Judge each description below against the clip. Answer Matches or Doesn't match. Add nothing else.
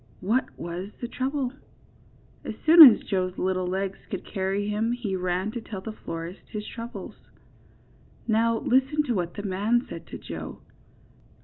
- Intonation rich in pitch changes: Doesn't match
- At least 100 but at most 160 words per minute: Matches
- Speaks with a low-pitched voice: Doesn't match